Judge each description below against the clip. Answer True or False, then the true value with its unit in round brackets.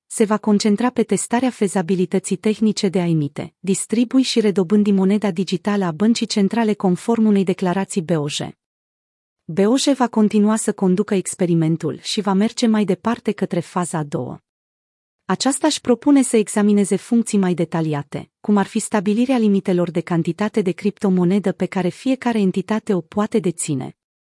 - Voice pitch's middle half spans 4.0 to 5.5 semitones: False (3.3 semitones)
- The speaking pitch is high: True (200 Hz)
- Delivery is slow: False (150 wpm)